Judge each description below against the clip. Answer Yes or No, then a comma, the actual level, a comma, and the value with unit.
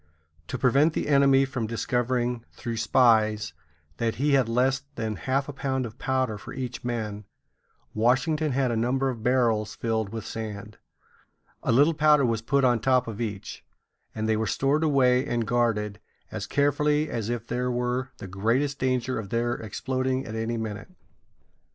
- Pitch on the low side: Yes, low, 120 Hz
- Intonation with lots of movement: No, average, 3.0 semitones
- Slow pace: No, average, 170 wpm